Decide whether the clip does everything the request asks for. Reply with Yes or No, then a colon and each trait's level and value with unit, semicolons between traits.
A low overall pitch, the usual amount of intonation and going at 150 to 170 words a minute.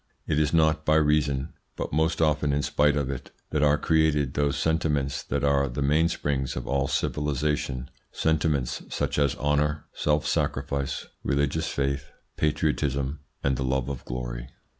No: very low, 70 Hz; narrow, 1.8 semitones; average, 155 wpm